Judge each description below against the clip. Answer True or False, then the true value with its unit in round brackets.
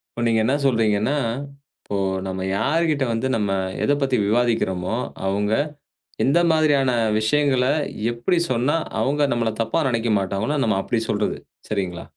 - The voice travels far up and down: False (4.5 semitones)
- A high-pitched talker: False (120 Hz)